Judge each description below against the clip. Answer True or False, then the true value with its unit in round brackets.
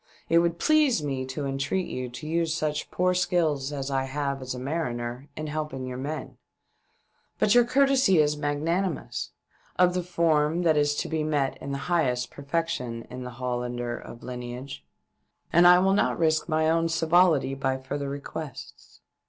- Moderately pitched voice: True (150 Hz)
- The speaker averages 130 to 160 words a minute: False (175 wpm)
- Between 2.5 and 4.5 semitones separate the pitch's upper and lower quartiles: True (4.2 semitones)